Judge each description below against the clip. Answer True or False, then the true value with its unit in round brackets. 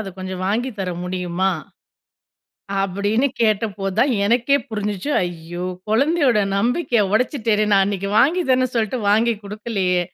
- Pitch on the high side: True (210 Hz)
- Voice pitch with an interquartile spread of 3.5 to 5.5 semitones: True (3.8 semitones)